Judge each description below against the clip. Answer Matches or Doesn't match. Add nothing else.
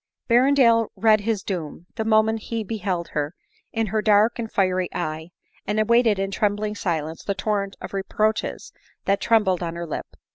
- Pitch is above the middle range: Matches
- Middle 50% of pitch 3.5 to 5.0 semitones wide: Doesn't match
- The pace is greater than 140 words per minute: Matches